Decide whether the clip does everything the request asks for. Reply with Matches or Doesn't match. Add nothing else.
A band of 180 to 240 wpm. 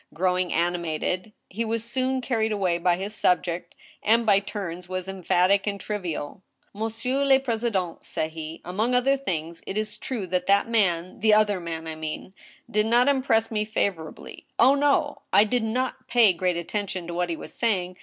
Matches